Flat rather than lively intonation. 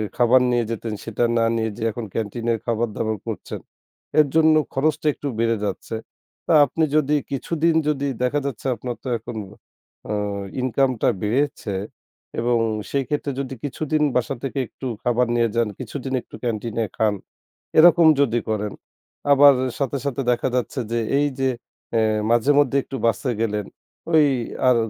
No: average, 3.6 semitones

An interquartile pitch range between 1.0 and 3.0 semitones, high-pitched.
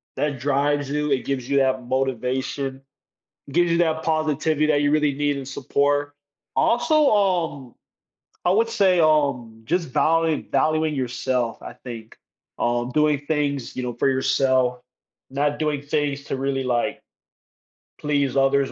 No: average, 2.7 semitones; medium, 140 Hz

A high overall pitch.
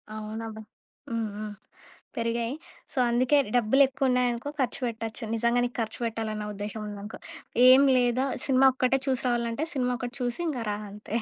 Yes: high, 235 Hz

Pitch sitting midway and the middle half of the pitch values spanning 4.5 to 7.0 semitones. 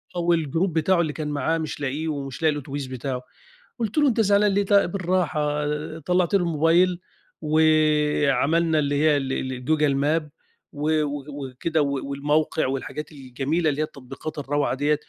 No: medium, 150 Hz; average, 2.7 semitones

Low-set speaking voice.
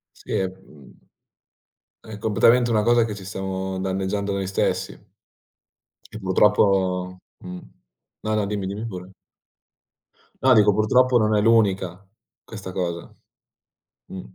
Yes: low, 100 Hz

